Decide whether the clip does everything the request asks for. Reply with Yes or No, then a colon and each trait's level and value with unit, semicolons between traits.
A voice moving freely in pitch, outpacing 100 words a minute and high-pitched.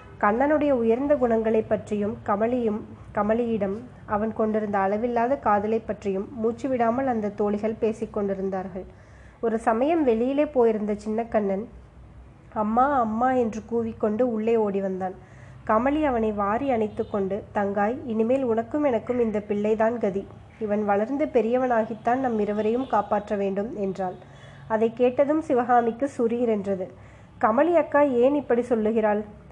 No: average, 2.7 semitones; average, 120 wpm; high, 225 Hz